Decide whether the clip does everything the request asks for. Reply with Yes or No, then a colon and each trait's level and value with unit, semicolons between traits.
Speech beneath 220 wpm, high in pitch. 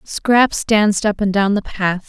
Yes: average, 200 wpm; high, 205 Hz